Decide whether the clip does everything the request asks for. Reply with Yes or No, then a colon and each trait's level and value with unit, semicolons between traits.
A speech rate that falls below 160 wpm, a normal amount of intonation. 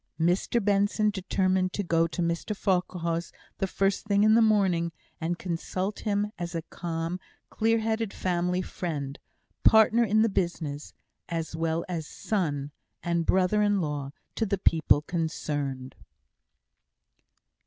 Yes: slow, 135 wpm; average, 3.7 semitones